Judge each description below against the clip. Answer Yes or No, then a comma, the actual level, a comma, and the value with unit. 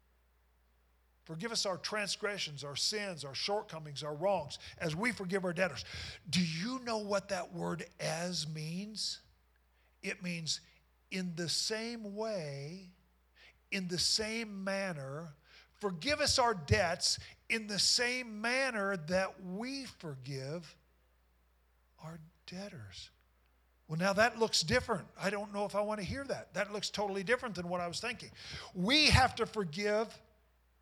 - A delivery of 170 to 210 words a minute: No, average, 140 wpm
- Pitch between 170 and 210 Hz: Yes, medium, 185 Hz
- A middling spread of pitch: No, wide, 6.6 semitones